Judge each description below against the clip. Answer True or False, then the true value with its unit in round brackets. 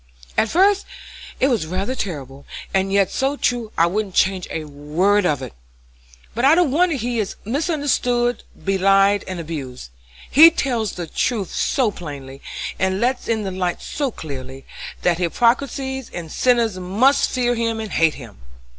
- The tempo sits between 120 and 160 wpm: True (155 wpm)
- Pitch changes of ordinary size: False (6.5 semitones)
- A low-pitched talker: False (205 Hz)